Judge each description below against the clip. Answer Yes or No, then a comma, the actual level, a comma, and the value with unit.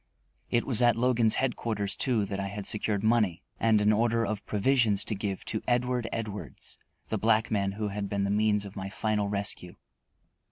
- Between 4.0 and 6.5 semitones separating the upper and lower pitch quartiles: No, narrow, 2.4 semitones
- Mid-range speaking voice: No, low, 105 Hz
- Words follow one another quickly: No, average, 190 wpm